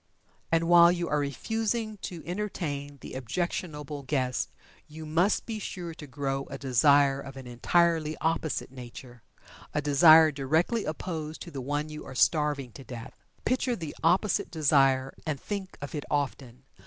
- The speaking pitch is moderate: Yes, medium, 150 Hz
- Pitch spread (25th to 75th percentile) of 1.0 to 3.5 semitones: No, average, 3.9 semitones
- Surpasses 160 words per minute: No, average, 155 wpm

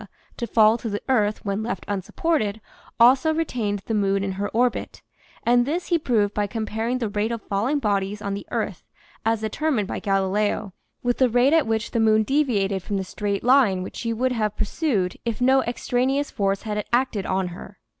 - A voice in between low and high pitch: No, high, 220 Hz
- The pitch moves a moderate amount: Yes, average, 3.6 semitones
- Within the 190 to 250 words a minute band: Yes, average, 195 wpm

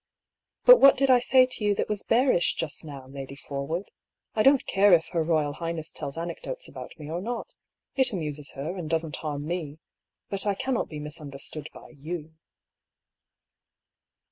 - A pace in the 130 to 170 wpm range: No, average, 180 wpm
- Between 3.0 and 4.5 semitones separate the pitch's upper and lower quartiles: No, wide, 5.6 semitones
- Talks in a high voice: No, medium, 165 Hz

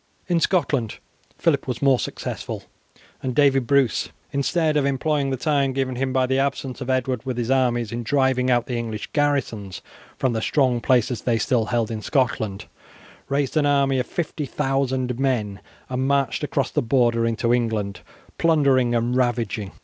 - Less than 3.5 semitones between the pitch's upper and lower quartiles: Yes, average, 2.8 semitones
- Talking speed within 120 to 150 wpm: No, average, 165 wpm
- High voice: No, low, 130 Hz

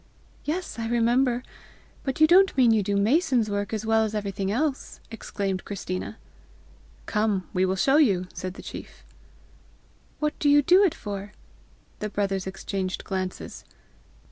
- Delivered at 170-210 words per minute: No, average, 150 wpm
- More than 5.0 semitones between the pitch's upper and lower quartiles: Yes, wide, 5.4 semitones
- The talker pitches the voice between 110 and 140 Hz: No, high, 215 Hz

